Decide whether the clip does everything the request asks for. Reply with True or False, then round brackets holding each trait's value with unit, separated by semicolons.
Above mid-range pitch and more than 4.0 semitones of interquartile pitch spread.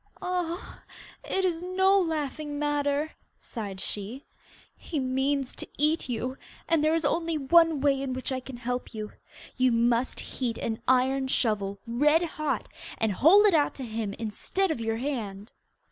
True (270 Hz; 5.2 semitones)